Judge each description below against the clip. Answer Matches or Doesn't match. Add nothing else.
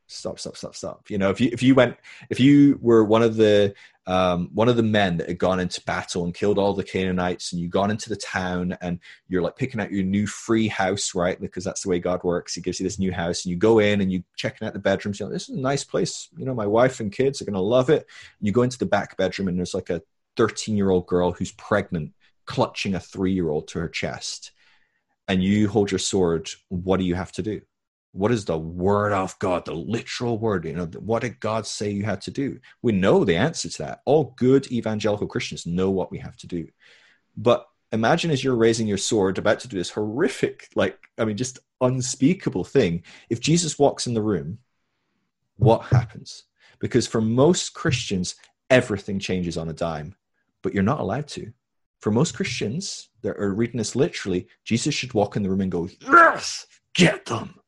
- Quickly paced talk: Matches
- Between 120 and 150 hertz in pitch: Doesn't match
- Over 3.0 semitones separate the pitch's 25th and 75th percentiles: Matches